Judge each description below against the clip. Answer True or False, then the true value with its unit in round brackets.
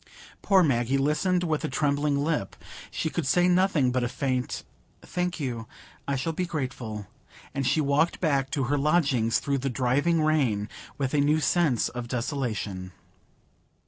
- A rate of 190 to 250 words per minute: False (160 wpm)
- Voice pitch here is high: False (140 Hz)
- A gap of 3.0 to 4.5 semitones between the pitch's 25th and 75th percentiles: True (3.9 semitones)